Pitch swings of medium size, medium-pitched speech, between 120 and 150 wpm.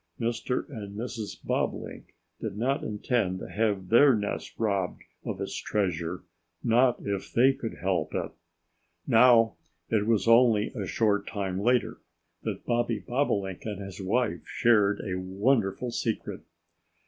No: average, 3.3 semitones; low, 110 Hz; slow, 135 wpm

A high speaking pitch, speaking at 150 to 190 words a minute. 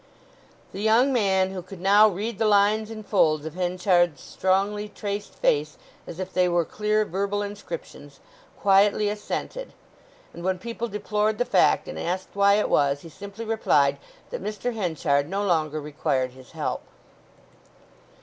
Yes: high, 200 Hz; average, 155 wpm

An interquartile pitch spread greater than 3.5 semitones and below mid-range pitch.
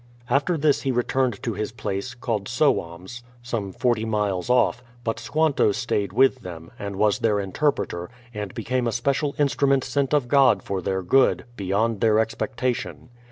Yes: average, 4.6 semitones; low, 115 Hz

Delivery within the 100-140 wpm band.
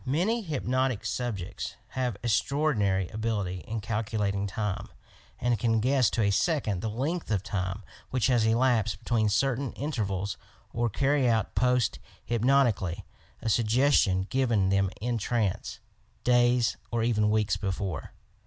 Yes: slow, 135 wpm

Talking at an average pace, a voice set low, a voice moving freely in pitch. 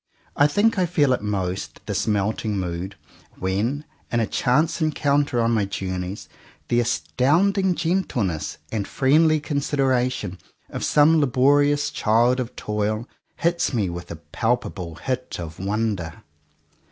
No: slow, 130 wpm; low, 120 Hz; wide, 6.7 semitones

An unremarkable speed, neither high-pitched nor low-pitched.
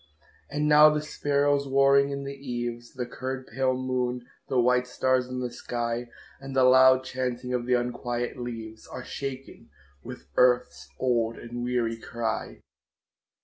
No: average, 150 wpm; low, 125 Hz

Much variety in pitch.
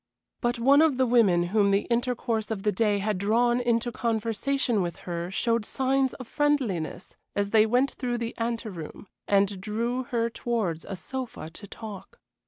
No: average, 3.4 semitones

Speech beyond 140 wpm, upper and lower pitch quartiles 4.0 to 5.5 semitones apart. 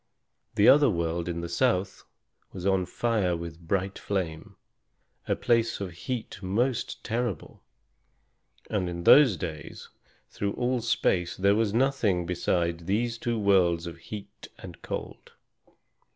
No: slow, 135 wpm; average, 4.8 semitones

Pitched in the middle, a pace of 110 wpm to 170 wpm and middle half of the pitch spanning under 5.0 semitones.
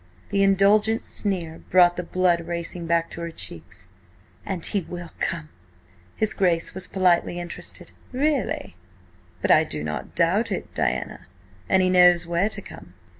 Yes: medium, 175 Hz; average, 155 wpm; narrow, 2.4 semitones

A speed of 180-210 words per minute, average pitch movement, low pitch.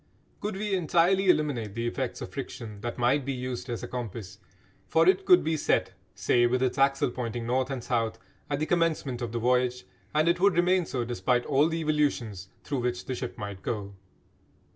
Yes: average, 200 wpm; average, 4.8 semitones; low, 125 Hz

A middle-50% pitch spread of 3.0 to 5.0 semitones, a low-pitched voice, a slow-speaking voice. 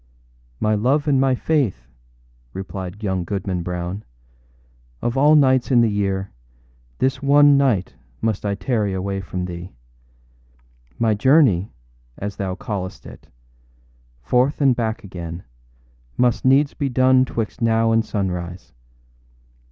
No: wide, 5.5 semitones; low, 110 Hz; slow, 130 wpm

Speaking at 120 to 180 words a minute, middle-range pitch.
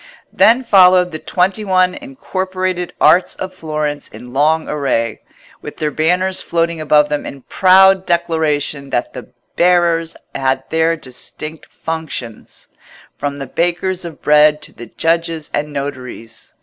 Yes: slow, 135 wpm; medium, 160 Hz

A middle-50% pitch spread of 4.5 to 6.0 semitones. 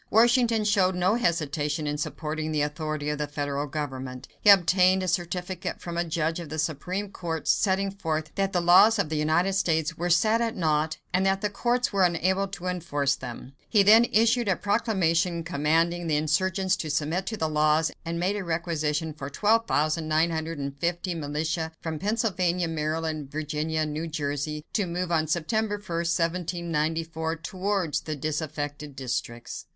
No: average, 3.5 semitones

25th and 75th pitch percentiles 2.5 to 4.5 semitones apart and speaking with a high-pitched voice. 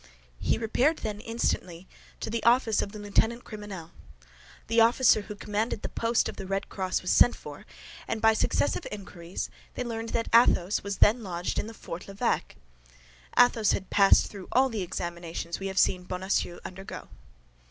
Yes: average, 3.4 semitones; high, 205 Hz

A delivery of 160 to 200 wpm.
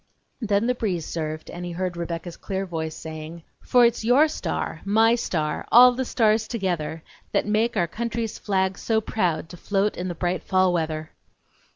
Yes: average, 180 wpm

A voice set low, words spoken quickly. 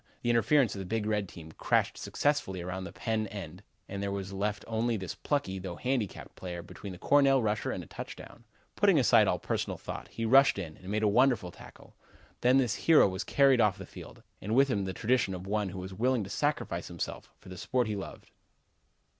Yes: low, 105 Hz; fast, 215 wpm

